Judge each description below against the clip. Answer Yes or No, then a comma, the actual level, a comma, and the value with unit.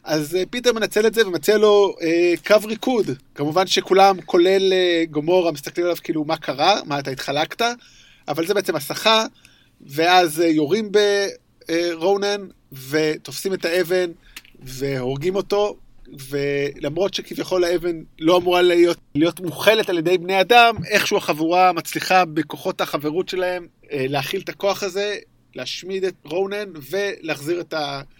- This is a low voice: No, medium, 175 Hz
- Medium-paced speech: Yes, average, 130 wpm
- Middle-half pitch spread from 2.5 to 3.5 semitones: No, average, 3.9 semitones